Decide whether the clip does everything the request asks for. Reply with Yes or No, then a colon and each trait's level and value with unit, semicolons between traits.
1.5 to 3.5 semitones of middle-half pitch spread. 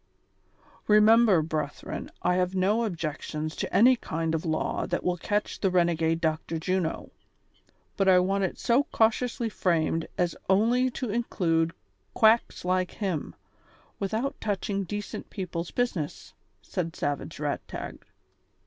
No: average, 4.7 semitones